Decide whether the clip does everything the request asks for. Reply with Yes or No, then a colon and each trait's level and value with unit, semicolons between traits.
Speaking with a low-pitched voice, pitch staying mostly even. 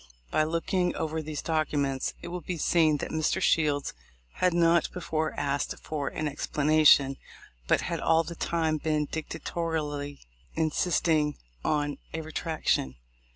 No: medium, 155 Hz; narrow, 2.0 semitones